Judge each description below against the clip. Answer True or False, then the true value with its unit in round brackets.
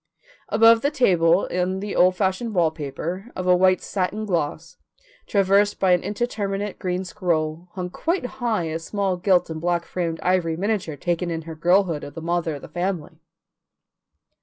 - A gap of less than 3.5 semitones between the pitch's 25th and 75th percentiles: True (3.1 semitones)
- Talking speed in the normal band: True (165 wpm)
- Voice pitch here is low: False (180 Hz)